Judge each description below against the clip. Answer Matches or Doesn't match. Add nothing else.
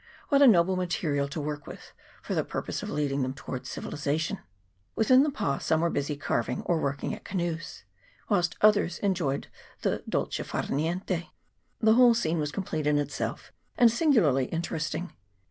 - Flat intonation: Doesn't match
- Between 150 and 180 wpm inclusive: Matches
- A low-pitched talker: Doesn't match